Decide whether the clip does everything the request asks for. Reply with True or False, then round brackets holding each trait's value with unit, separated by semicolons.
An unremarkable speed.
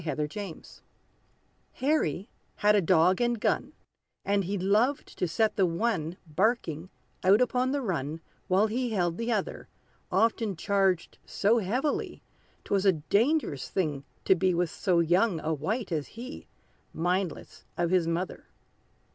True (145 wpm)